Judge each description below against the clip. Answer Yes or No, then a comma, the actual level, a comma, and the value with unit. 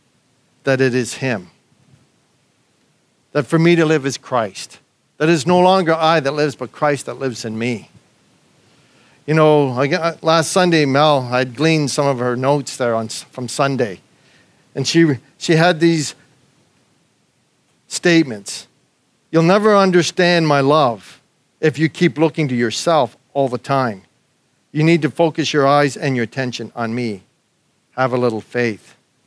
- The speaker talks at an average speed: Yes, average, 155 wpm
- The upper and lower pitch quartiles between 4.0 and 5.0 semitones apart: Yes, average, 4.4 semitones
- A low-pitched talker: No, medium, 145 Hz